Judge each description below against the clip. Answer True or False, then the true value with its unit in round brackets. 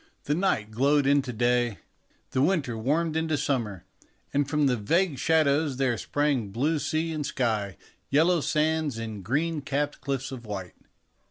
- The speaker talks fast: False (155 wpm)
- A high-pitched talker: False (140 Hz)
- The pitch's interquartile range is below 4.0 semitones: False (4.4 semitones)